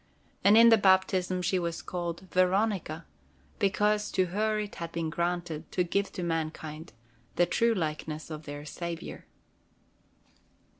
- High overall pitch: No, medium, 175 Hz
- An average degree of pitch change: Yes, average, 3.3 semitones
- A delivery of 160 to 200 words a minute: No, average, 140 wpm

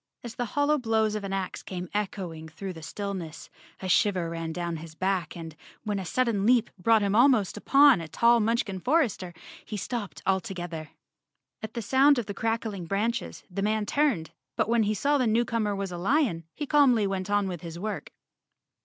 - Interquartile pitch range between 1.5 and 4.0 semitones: No, average, 4.4 semitones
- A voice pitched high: Yes, high, 205 Hz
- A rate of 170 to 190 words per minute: No, average, 200 wpm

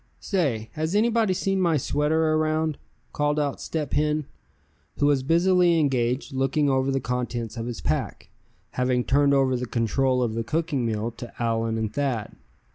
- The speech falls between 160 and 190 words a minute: Yes, average, 165 wpm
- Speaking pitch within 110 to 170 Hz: Yes, medium, 140 Hz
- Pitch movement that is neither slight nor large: Yes, average, 4.4 semitones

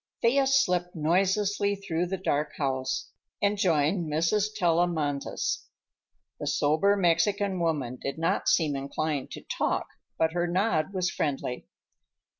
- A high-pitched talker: No, medium, 170 Hz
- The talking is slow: Yes, slow, 125 wpm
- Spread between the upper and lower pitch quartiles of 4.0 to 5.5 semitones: Yes, average, 4.4 semitones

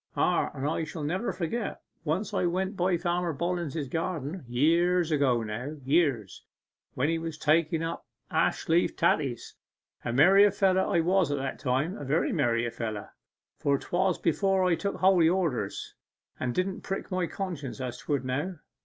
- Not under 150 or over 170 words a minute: Yes, average, 165 wpm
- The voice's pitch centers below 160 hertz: No, medium, 165 Hz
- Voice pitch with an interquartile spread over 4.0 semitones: Yes, average, 5.0 semitones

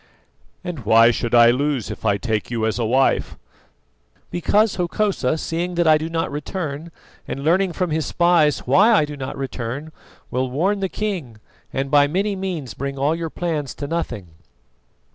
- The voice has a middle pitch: Yes, medium, 150 Hz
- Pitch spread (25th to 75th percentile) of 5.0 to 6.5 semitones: Yes, average, 5.3 semitones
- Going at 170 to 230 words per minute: Yes, average, 175 wpm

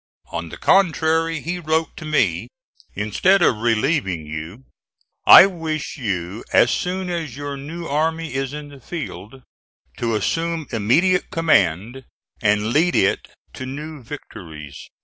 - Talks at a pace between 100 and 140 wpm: Yes, slow, 135 wpm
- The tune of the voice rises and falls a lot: Yes, wide, 7.3 semitones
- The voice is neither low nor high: Yes, medium, 145 Hz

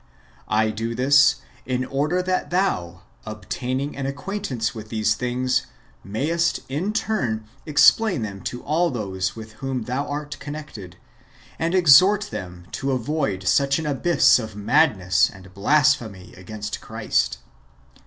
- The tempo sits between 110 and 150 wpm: Yes, average, 140 wpm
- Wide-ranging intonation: Yes, wide, 5.8 semitones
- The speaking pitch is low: Yes, low, 130 Hz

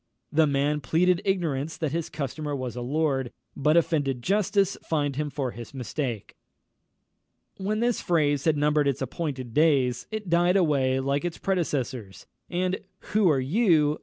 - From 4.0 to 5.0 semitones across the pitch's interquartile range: Yes, average, 4.3 semitones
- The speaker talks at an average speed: Yes, average, 155 wpm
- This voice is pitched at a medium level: Yes, medium, 150 Hz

